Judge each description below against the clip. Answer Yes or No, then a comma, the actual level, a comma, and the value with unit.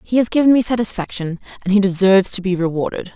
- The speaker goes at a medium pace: No, fast, 210 wpm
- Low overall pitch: No, high, 200 Hz